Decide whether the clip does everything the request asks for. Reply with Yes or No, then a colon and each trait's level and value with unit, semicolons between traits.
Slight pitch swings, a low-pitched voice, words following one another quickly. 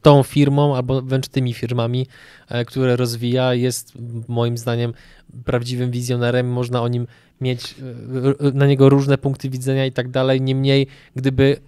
No: narrow, 1.8 semitones; low, 130 Hz; average, 140 wpm